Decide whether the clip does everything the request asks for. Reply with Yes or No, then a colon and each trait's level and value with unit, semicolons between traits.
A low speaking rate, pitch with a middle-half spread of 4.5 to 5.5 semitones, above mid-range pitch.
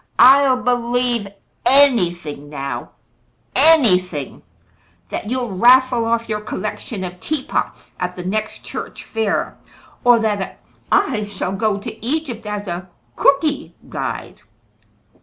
Yes: slow, 115 wpm; average, 5.2 semitones; high, 220 Hz